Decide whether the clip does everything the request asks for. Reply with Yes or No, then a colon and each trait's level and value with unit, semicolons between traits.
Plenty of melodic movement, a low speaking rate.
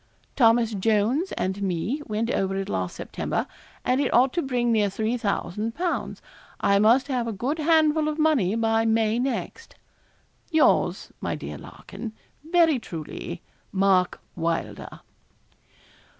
Yes: wide, 5.8 semitones; slow, 130 wpm